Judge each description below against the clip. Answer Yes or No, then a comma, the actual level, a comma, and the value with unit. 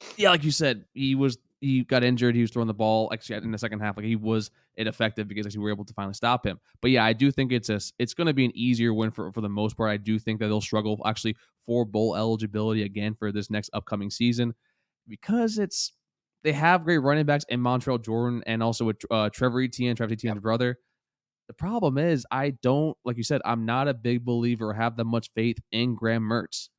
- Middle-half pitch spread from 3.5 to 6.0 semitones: No, average, 2.7 semitones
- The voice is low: Yes, low, 115 Hz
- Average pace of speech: No, fast, 235 wpm